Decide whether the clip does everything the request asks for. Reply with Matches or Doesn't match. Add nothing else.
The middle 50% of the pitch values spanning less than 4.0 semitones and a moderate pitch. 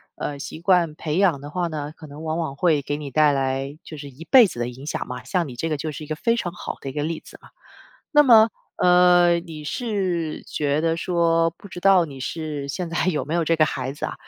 Matches